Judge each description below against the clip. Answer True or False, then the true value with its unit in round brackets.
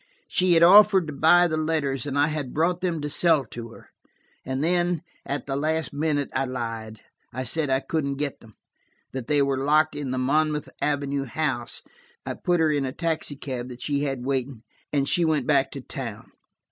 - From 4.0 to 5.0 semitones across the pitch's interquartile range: False (3.1 semitones)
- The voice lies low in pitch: False (145 Hz)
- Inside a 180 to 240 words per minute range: True (195 wpm)